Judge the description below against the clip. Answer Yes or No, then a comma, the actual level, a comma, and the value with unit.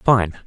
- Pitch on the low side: Yes, low, 105 Hz